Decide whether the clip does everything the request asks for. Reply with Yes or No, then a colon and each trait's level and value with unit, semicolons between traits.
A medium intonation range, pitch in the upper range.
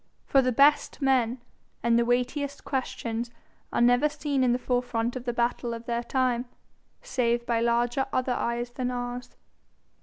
No: narrow, 1.5 semitones; high, 245 Hz